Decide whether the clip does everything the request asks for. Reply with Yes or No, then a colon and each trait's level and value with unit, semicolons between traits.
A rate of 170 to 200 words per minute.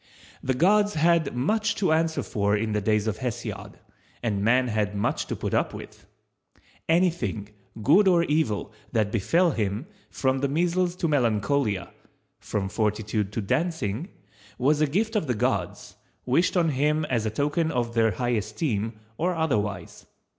No: average, 155 wpm